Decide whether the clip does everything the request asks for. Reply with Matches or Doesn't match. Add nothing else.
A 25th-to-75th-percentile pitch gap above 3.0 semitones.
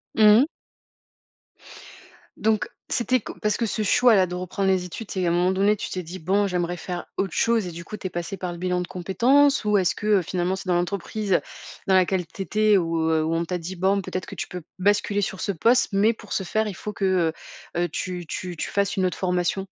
Doesn't match